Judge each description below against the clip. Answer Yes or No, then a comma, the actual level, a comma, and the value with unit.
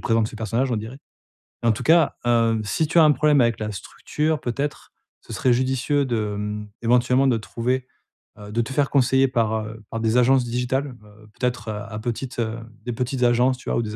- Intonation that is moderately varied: Yes, average, 3.0 semitones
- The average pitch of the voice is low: Yes, low, 120 Hz